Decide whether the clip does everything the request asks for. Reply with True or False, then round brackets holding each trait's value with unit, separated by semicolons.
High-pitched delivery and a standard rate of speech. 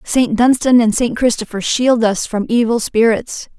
True (230 Hz; 165 wpm)